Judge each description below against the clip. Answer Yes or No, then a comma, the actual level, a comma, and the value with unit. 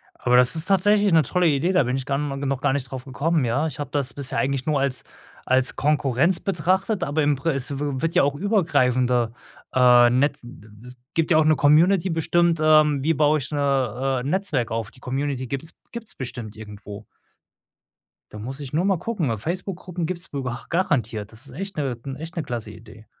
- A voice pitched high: No, medium, 140 Hz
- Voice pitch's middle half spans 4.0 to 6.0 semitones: Yes, average, 4.5 semitones